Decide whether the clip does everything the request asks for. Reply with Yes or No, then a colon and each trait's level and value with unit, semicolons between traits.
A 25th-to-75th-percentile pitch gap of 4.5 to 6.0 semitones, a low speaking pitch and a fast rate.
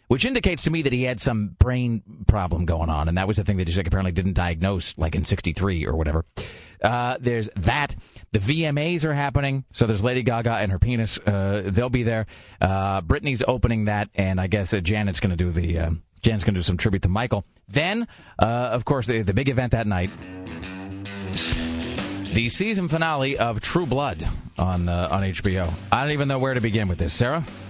Yes: average, 5.0 semitones; low, 105 Hz; fast, 210 wpm